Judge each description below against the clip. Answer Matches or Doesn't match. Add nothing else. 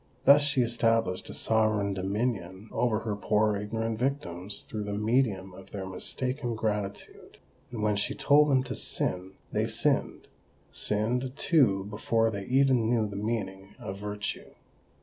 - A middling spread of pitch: Matches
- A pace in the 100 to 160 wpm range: Matches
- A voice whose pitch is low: Matches